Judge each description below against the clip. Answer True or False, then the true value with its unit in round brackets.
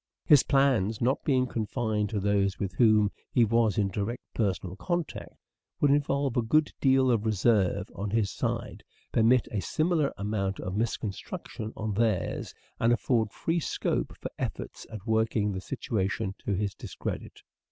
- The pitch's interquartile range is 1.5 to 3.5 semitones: False (3.9 semitones)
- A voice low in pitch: True (110 Hz)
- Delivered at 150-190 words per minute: True (160 wpm)